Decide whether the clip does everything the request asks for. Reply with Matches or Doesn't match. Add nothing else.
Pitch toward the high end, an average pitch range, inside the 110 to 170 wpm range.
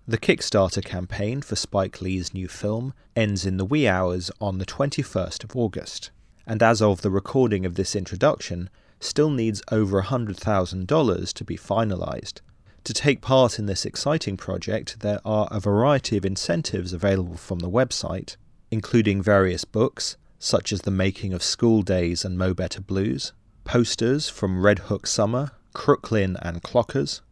Doesn't match